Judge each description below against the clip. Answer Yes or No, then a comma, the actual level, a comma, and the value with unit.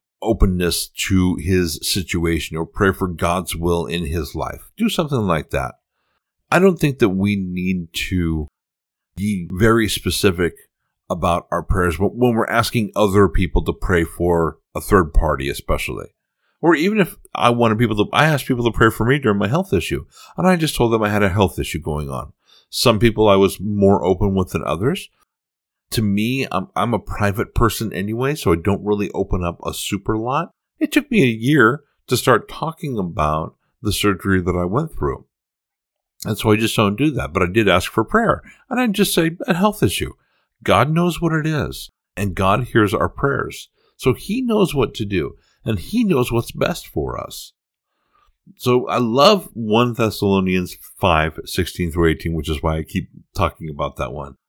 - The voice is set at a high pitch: No, low, 105 Hz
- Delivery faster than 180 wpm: Yes, average, 190 wpm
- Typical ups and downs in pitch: No, wide, 5.9 semitones